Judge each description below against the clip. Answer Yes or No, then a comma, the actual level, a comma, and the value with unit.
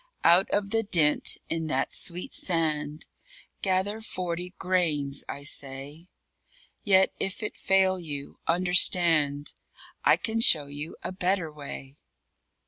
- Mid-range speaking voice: Yes, medium, 170 Hz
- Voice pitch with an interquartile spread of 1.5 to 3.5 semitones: No, average, 4.1 semitones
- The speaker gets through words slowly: Yes, slow, 125 wpm